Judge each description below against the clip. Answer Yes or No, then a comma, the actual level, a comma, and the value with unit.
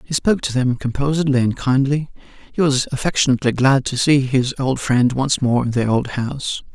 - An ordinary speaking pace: Yes, average, 195 wpm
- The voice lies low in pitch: Yes, low, 130 Hz